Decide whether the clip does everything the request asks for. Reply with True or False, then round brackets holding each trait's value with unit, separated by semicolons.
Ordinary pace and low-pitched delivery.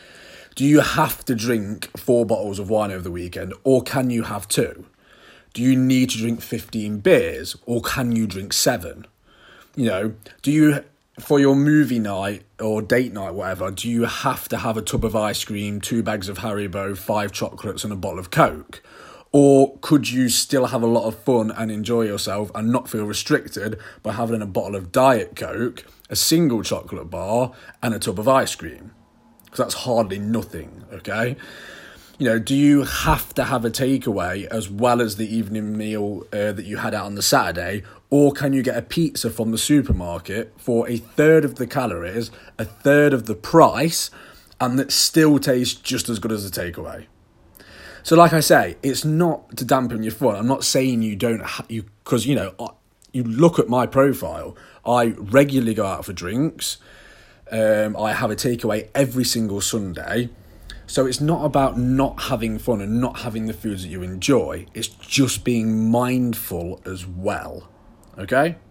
True (190 wpm; 115 Hz)